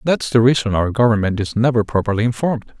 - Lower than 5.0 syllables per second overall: No, 6.4 syllables/s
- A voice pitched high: No, low, 115 Hz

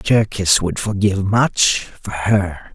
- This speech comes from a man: Yes, male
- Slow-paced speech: Yes, slow, 130 wpm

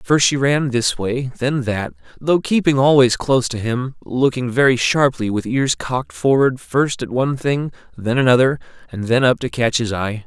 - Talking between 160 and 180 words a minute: No, average, 195 wpm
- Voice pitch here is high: No, low, 130 Hz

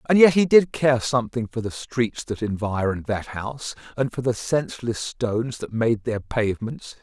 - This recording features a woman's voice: No, male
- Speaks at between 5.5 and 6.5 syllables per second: No, 5.0 syllables/s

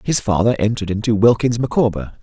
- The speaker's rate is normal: Yes, average, 160 wpm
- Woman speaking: No, male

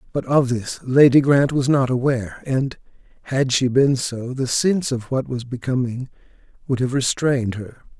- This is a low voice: Yes, low, 130 Hz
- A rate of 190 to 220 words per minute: No, average, 175 wpm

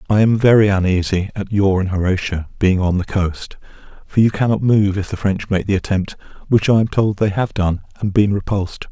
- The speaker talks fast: Yes, fast, 215 wpm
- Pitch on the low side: Yes, low, 100 Hz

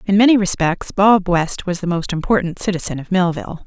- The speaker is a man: No, female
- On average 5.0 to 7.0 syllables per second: Yes, 5.6 syllables/s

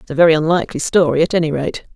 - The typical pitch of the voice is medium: Yes, medium, 160 Hz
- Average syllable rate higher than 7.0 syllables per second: Yes, 7.5 syllables/s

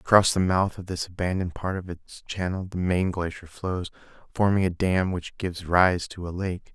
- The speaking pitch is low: Yes, very low, 90 Hz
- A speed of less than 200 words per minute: No, fast, 205 wpm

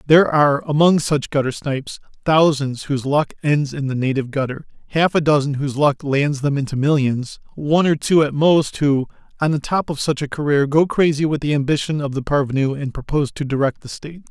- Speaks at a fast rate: Yes, fast, 210 wpm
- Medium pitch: Yes, medium, 145 Hz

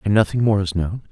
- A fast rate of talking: Yes, fast, 270 wpm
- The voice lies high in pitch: No, low, 100 Hz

